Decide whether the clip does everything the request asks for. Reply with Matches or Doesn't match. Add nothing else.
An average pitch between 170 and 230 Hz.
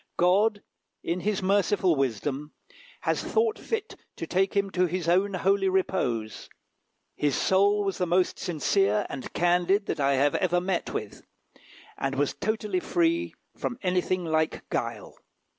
Matches